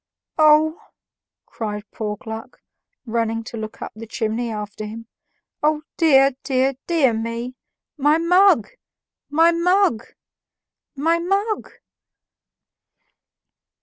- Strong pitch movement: Yes, wide, 6.5 semitones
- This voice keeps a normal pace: No, slow, 100 wpm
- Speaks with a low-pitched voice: No, very high, 265 Hz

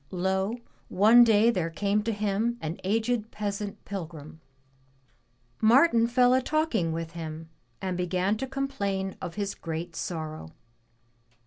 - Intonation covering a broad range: No, average, 5.0 semitones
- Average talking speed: No, slow, 130 wpm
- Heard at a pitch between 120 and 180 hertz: No, high, 200 Hz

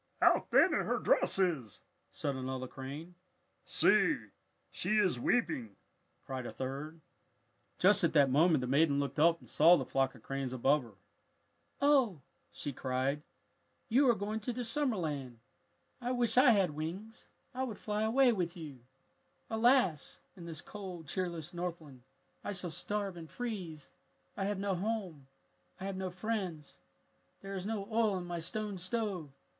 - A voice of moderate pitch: Yes, medium, 175 Hz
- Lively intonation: Yes, wide, 6.4 semitones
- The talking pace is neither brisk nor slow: Yes, average, 160 wpm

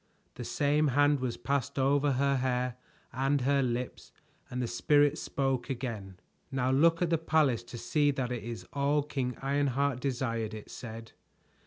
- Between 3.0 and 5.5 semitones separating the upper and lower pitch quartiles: No, narrow, 2.6 semitones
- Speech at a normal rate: Yes, average, 165 wpm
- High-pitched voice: No, low, 135 Hz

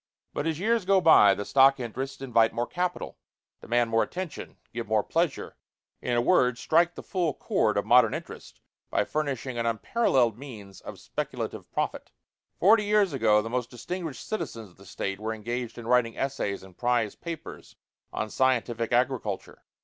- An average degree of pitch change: No, wide, 6.0 semitones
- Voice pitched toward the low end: Yes, low, 125 Hz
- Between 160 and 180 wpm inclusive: Yes, average, 170 wpm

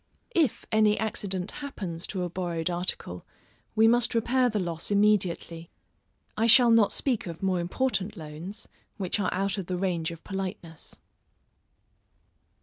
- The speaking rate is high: No, average, 145 wpm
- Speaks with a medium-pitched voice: No, high, 195 Hz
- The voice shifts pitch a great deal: No, average, 4.1 semitones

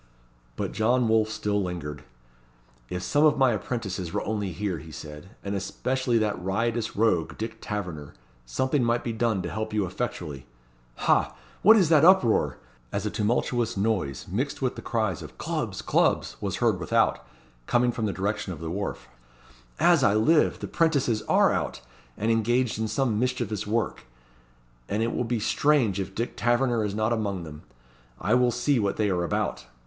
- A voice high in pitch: No, low, 110 Hz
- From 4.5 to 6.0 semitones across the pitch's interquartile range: No, average, 3.9 semitones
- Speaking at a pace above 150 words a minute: Yes, average, 175 wpm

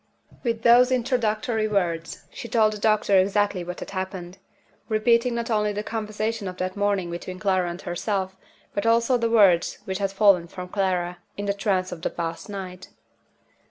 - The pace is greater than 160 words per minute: Yes, average, 175 wpm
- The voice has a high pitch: Yes, high, 200 Hz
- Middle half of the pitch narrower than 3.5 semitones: Yes, average, 3.0 semitones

